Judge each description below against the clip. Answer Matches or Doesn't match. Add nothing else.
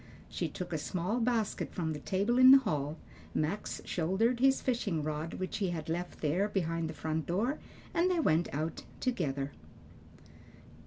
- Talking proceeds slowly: Doesn't match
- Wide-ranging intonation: Matches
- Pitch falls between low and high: Matches